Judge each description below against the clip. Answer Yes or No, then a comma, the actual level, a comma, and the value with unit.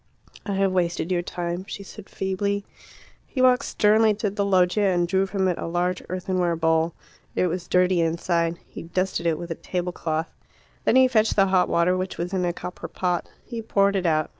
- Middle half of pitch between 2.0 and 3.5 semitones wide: Yes, narrow, 2.4 semitones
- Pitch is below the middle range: No, medium, 185 Hz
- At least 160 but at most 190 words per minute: No, average, 200 wpm